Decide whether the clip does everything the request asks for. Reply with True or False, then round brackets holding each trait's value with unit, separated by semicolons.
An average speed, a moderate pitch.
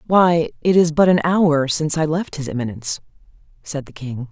True (195 wpm; 150 Hz)